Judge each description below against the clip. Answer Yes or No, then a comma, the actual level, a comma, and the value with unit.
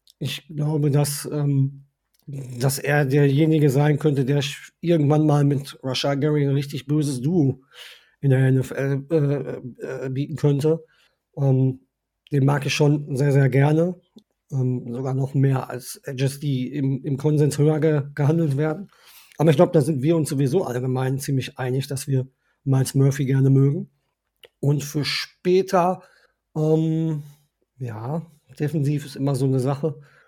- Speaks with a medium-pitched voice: Yes, medium, 145 Hz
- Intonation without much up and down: Yes, narrow, 2.1 semitones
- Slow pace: No, average, 150 wpm